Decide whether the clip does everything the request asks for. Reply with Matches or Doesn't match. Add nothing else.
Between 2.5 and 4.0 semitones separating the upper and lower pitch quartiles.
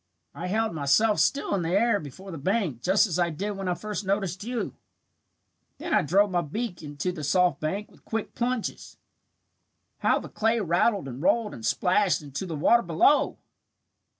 Doesn't match